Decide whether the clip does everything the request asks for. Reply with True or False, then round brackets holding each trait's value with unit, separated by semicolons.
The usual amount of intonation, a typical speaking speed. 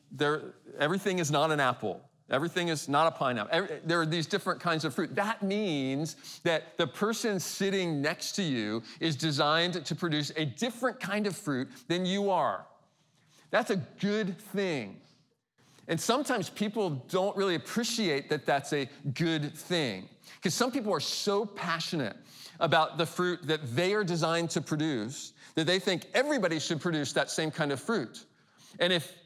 True (4.1 semitones; 170 wpm)